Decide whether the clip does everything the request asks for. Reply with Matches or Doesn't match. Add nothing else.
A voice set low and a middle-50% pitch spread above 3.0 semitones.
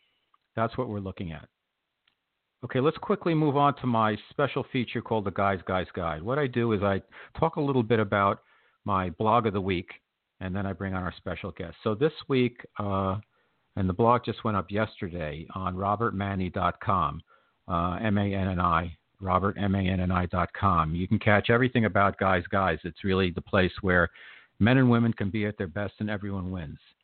Matches